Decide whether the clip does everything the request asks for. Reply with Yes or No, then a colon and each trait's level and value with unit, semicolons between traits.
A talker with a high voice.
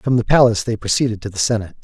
No: low, 110 Hz